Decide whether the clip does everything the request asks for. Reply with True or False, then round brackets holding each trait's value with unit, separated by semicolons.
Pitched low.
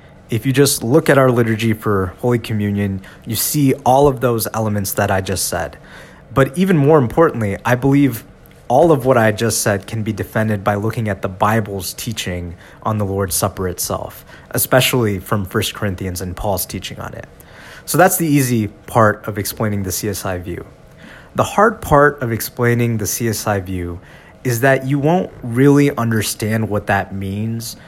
True (110 Hz)